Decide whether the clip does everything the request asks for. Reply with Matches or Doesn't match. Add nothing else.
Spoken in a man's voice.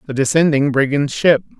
Matches